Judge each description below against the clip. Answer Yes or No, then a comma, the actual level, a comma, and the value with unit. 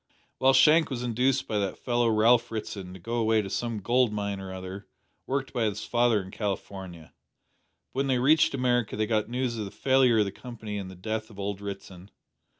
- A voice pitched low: Yes, low, 110 Hz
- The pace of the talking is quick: Yes, fast, 210 wpm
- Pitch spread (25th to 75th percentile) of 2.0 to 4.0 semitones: Yes, average, 3.5 semitones